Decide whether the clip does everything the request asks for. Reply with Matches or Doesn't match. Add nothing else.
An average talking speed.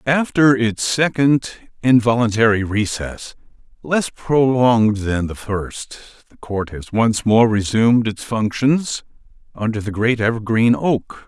Doesn't match